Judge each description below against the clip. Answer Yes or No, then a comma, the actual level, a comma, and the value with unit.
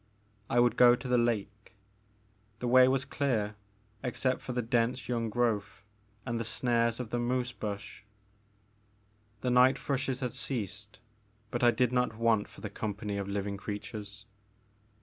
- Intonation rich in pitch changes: No, average, 2.9 semitones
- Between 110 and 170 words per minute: Yes, average, 155 wpm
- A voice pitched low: Yes, low, 120 Hz